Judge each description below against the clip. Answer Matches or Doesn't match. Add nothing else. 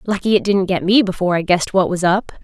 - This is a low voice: Doesn't match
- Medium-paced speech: Doesn't match